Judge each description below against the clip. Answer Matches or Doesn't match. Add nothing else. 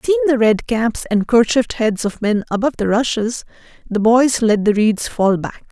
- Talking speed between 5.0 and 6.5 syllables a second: Matches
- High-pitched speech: Matches